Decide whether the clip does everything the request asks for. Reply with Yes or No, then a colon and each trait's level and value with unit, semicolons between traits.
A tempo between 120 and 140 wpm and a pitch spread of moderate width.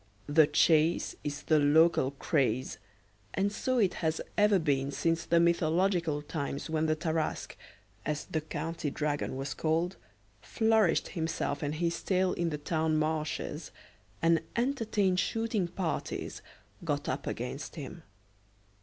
Yes: slow, 135 wpm; average, 3.2 semitones